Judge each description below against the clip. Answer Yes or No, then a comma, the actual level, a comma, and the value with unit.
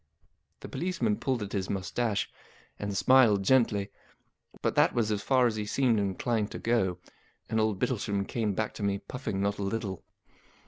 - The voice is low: Yes, low, 105 Hz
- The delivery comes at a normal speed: Yes, average, 180 wpm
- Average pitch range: Yes, average, 3.0 semitones